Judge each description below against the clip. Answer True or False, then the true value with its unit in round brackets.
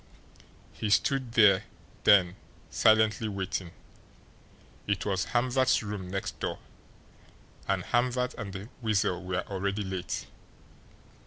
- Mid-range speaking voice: False (100 Hz)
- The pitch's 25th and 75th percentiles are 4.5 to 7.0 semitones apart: False (3.0 semitones)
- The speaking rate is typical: False (105 wpm)